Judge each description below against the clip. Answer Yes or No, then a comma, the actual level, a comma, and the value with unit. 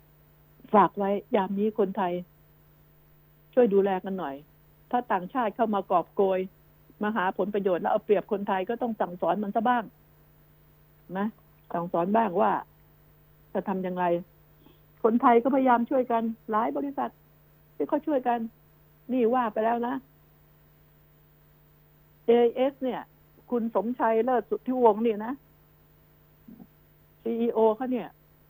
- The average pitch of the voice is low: No, high, 205 Hz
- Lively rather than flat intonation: Yes, wide, 7.4 semitones